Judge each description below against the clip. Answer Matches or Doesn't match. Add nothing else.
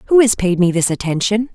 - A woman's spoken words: Matches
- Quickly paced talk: Matches